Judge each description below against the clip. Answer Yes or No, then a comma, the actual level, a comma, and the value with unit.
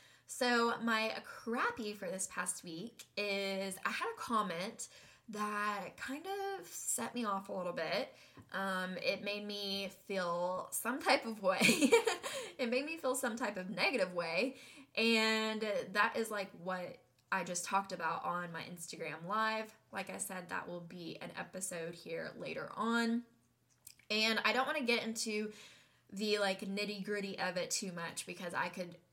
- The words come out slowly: No, average, 165 wpm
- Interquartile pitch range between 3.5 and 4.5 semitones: Yes, average, 4.1 semitones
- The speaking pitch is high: Yes, high, 205 Hz